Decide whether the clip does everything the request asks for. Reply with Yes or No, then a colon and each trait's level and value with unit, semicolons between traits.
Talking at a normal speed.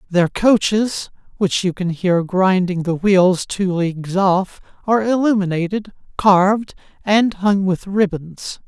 No: slow, 130 wpm